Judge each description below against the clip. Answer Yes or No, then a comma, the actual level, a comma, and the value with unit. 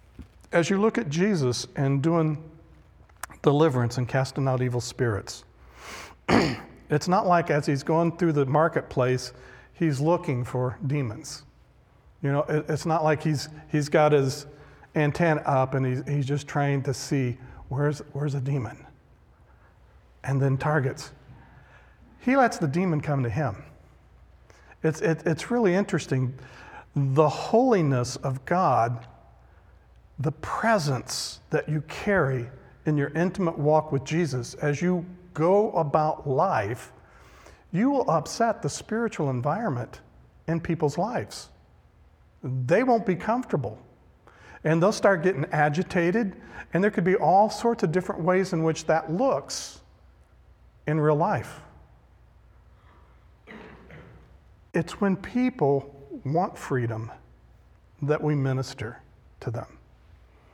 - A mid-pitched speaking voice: Yes, medium, 150 Hz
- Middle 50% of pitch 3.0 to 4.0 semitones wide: No, average, 4.8 semitones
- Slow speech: Yes, slow, 125 wpm